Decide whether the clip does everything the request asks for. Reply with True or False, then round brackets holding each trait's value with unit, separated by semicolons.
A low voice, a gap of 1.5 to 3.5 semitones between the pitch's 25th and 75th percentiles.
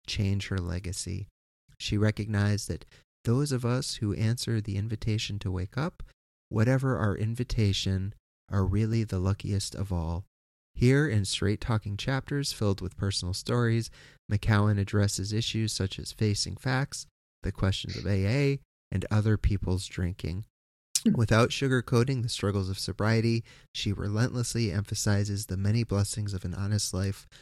True (105 Hz; 3.1 semitones)